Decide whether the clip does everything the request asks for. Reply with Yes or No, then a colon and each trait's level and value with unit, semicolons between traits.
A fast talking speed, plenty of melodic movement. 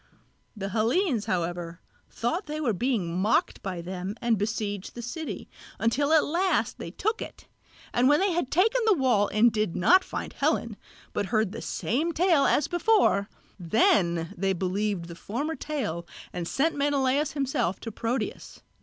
No: average, 165 wpm; wide, 7.7 semitones